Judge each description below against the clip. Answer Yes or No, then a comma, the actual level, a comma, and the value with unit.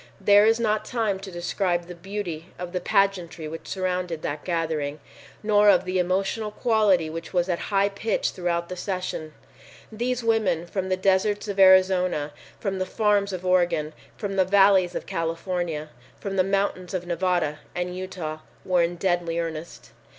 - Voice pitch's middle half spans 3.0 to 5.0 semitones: No, narrow, 2.5 semitones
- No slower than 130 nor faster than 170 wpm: Yes, average, 165 wpm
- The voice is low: No, medium, 185 Hz